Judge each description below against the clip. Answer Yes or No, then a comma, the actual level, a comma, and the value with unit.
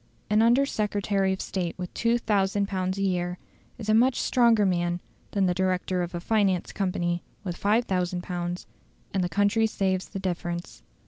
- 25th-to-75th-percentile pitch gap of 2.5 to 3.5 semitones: Yes, average, 2.8 semitones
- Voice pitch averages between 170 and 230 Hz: Yes, high, 190 Hz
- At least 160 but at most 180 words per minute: Yes, average, 170 wpm